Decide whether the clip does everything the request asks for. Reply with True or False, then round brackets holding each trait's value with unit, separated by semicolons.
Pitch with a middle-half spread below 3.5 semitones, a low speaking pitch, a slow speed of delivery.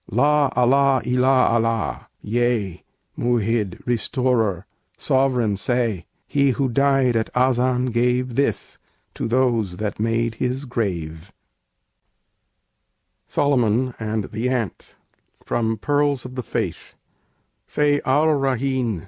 True (2.8 semitones; 125 Hz; 105 wpm)